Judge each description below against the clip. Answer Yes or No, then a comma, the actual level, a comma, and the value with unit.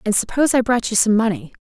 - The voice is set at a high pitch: Yes, high, 220 Hz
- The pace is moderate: No, fast, 255 wpm